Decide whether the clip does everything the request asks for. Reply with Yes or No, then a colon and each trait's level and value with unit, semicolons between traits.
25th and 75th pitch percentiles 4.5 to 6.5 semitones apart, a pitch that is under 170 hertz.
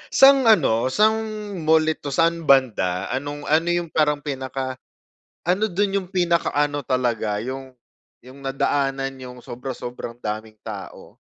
Yes: average, 4.9 semitones; medium, 140 Hz